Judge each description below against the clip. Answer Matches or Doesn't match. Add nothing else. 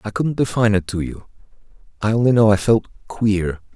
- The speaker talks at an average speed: Matches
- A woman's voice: Doesn't match